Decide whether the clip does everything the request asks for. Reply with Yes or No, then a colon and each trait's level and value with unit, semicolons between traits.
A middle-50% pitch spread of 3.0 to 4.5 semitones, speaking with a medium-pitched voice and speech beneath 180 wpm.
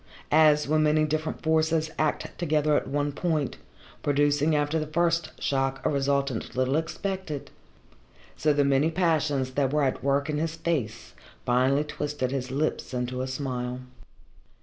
No: narrow, 2.6 semitones; medium, 145 Hz; average, 150 wpm